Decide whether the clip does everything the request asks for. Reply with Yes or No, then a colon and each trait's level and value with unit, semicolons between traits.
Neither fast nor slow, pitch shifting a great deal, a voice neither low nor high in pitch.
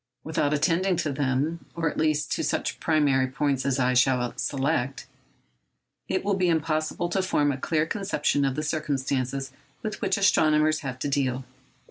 No: average, 155 wpm; average, 3.4 semitones; medium, 150 Hz